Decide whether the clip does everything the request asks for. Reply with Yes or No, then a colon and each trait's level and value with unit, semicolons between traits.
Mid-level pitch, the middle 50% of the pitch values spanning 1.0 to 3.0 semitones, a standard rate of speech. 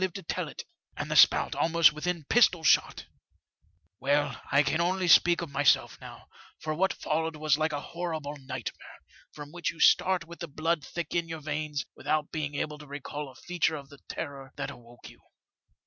Yes: medium, 155 Hz; average, 2.7 semitones; average, 195 wpm